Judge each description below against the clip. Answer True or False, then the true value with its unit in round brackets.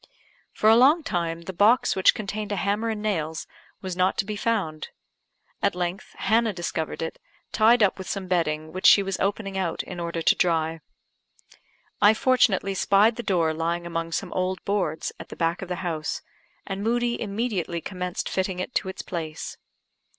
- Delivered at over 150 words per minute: True (180 wpm)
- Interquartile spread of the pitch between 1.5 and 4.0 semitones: True (3.7 semitones)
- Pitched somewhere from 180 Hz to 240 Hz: True (190 Hz)